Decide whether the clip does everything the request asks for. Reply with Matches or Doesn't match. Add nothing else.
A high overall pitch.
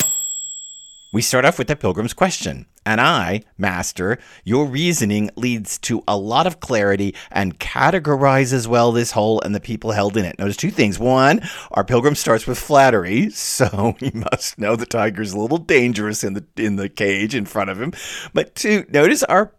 Doesn't match